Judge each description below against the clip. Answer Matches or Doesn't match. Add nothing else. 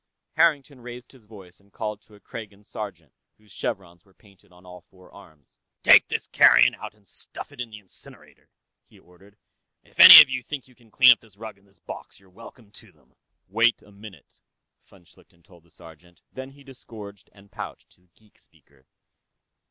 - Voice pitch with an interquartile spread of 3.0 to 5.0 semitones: Matches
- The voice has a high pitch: Doesn't match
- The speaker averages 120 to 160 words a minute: Doesn't match